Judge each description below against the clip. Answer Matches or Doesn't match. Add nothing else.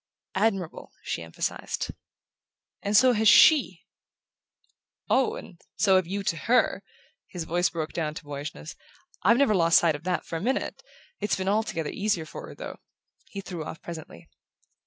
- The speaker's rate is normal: Matches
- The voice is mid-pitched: Matches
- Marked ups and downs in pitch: Doesn't match